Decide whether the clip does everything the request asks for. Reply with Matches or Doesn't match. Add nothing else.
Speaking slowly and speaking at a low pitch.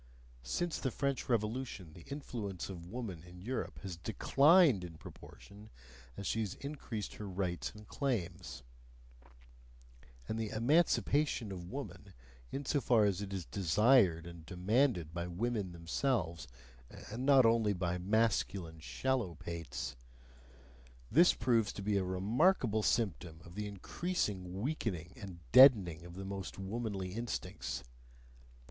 Matches